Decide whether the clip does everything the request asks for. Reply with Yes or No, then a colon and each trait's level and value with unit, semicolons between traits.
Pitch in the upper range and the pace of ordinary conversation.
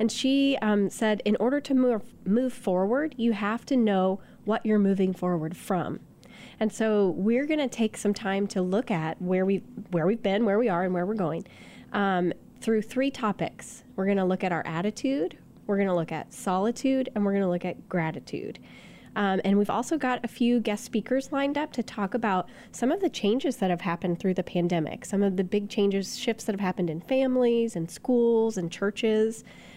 No: high, 210 Hz; fast, 210 wpm